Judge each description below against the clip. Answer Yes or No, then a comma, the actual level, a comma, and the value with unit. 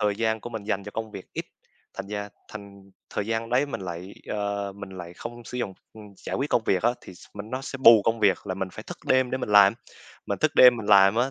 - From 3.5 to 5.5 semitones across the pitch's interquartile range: No, average, 2.8 semitones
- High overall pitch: No, low, 105 Hz